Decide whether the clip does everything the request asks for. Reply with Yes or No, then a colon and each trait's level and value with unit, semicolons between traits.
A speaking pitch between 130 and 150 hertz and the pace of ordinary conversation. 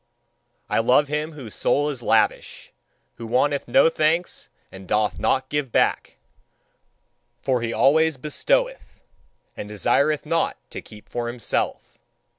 No: medium, 140 Hz; slow, 130 wpm